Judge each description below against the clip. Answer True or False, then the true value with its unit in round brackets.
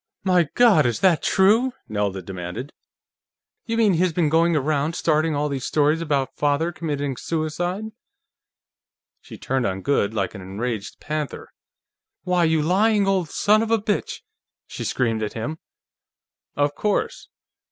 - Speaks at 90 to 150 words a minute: True (145 wpm)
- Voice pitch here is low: False (155 Hz)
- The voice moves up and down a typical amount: False (5.7 semitones)